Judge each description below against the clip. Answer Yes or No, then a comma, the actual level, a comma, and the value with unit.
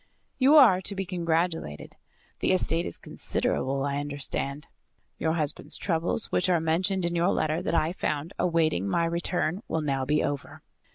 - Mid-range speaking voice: Yes, medium, 165 Hz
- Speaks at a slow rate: No, average, 165 wpm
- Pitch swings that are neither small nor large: Yes, average, 3.4 semitones